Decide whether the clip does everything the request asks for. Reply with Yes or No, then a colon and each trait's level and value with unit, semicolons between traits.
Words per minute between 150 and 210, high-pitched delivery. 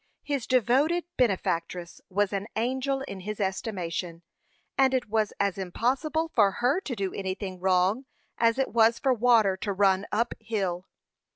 Yes: average, 155 wpm; high, 215 Hz